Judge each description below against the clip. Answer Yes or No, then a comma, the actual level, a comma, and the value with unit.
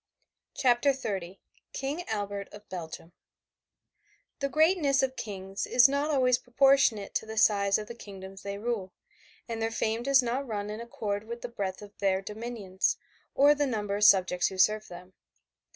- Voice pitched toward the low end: No, high, 215 Hz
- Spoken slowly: No, average, 170 wpm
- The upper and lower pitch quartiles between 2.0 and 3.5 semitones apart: No, average, 4.1 semitones